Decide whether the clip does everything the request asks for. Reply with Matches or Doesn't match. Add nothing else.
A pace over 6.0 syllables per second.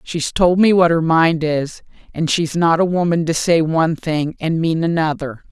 Doesn't match